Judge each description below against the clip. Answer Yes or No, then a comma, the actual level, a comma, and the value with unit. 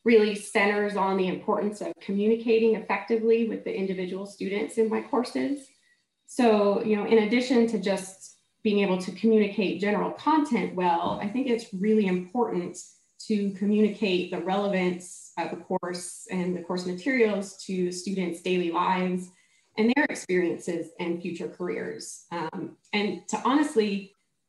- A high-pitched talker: Yes, high, 200 Hz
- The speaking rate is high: No, average, 145 wpm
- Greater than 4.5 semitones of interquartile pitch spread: No, average, 3.5 semitones